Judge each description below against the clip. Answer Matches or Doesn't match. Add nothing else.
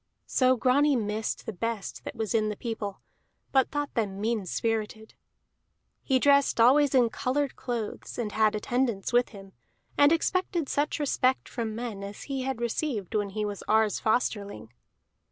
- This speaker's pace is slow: Doesn't match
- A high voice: Matches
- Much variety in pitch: Doesn't match